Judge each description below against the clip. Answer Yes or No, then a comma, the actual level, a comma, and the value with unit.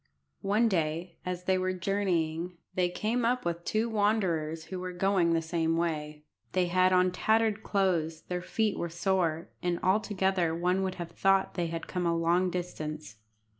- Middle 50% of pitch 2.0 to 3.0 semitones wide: Yes, narrow, 2.5 semitones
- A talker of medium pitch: Yes, medium, 180 Hz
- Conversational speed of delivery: Yes, average, 170 wpm